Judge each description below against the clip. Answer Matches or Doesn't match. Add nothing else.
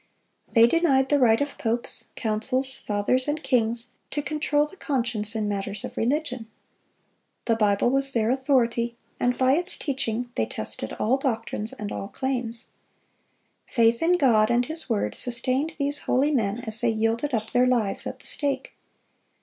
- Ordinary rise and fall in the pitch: Matches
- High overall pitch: Matches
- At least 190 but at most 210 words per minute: Doesn't match